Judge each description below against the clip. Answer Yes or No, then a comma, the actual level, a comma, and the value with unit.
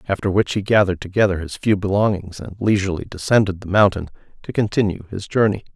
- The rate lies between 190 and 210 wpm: No, average, 175 wpm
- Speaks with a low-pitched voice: Yes, very low, 95 Hz